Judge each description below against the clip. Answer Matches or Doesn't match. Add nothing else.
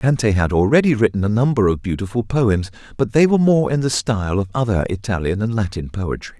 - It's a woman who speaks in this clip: Doesn't match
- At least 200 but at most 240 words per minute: Matches